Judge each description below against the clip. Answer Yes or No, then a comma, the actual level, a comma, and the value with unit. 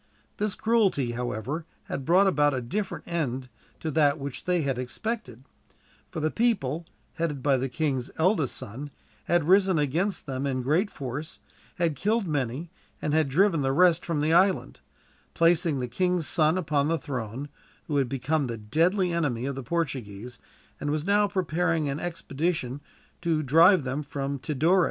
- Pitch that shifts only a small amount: No, average, 4.5 semitones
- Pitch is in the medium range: Yes, medium, 150 Hz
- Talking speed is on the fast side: No, average, 165 wpm